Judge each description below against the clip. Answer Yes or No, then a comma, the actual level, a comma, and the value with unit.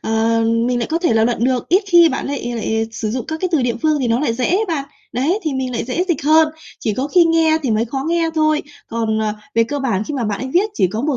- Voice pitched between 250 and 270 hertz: Yes, very high, 260 Hz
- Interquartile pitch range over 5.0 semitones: Yes, wide, 5.6 semitones